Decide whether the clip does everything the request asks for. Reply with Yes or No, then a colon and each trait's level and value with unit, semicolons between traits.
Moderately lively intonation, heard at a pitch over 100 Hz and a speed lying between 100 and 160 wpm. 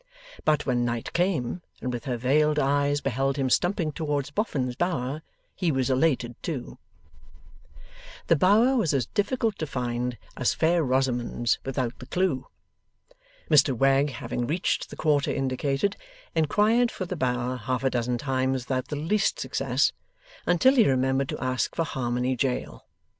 Yes: average, 4.2 semitones; low, 135 Hz; average, 155 wpm